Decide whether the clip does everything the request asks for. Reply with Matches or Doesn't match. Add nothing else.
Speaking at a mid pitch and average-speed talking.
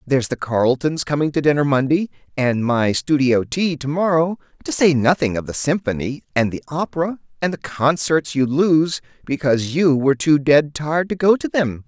Matches